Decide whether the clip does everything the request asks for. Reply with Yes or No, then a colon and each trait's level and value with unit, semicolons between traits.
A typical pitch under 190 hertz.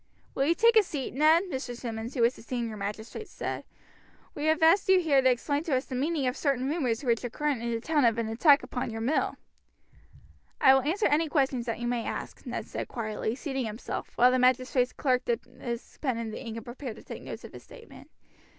No: very high, 255 Hz